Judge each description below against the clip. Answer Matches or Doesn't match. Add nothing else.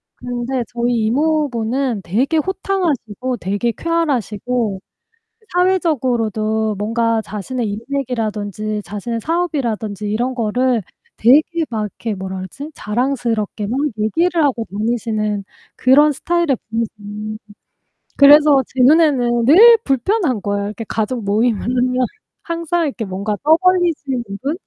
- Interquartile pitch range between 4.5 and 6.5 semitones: Matches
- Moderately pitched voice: Doesn't match